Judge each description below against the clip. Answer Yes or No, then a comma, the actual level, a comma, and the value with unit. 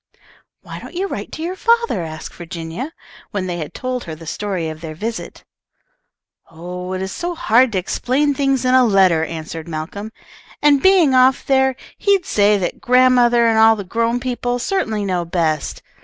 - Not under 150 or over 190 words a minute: Yes, average, 180 wpm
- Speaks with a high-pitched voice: Yes, high, 220 Hz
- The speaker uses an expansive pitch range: Yes, wide, 6.9 semitones